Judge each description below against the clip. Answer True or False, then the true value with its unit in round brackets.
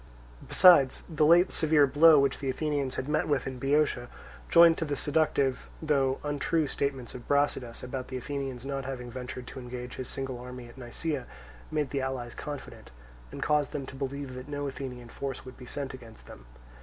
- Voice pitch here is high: False (135 Hz)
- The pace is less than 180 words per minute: False (190 wpm)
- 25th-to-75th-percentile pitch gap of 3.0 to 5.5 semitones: False (2.4 semitones)